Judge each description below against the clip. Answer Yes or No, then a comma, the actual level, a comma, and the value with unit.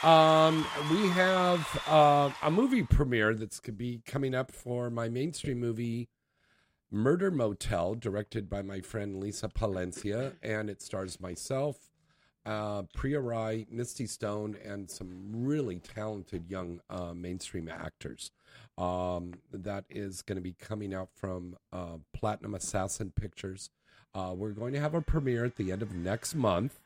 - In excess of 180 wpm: No, average, 150 wpm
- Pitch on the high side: No, low, 110 Hz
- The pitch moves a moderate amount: No, wide, 5.7 semitones